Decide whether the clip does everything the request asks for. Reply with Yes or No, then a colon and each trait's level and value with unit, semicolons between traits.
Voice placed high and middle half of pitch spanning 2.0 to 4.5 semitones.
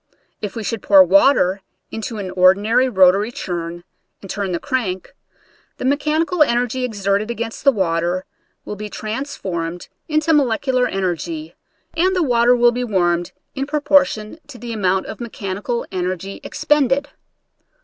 No: high, 220 Hz; wide, 5.6 semitones